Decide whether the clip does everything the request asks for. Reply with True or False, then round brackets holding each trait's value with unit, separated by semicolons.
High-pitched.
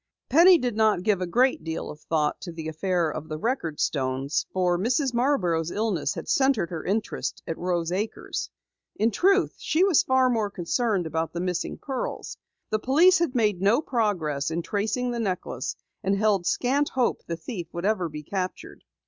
True (200 Hz)